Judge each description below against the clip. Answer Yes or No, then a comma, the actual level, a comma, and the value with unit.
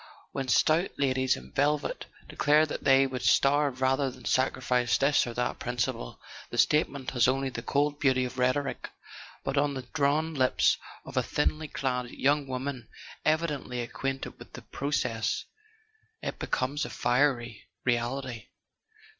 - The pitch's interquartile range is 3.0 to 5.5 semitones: No, narrow, 2.5 semitones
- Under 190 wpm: Yes, average, 150 wpm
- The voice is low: Yes, low, 130 Hz